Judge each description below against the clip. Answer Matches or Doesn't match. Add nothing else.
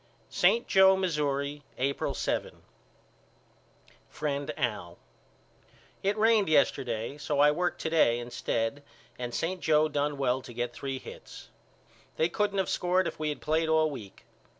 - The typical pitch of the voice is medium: Matches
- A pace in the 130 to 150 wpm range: Matches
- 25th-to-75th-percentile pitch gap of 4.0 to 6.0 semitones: Matches